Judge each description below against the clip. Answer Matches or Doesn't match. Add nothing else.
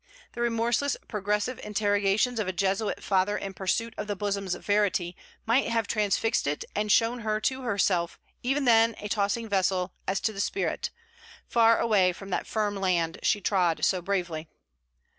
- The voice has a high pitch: Matches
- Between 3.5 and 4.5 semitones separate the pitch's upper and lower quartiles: Doesn't match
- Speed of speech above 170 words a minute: Doesn't match